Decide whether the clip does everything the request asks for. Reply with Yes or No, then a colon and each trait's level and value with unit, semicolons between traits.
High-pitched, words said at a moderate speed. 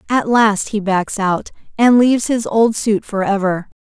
Yes: high, 210 Hz; average, 190 wpm